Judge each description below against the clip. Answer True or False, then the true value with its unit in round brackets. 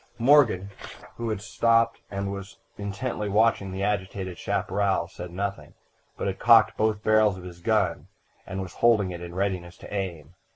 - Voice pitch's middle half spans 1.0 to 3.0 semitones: True (2.5 semitones)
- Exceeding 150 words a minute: True (165 wpm)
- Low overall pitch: True (100 Hz)